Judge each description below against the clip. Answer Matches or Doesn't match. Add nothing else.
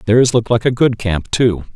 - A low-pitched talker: Matches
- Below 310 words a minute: Matches